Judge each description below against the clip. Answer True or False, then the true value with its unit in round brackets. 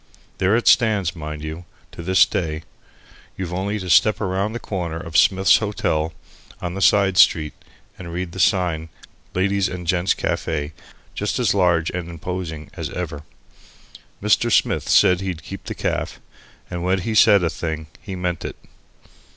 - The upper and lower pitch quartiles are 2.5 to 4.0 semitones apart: True (2.9 semitones)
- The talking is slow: False (165 wpm)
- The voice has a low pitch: True (90 Hz)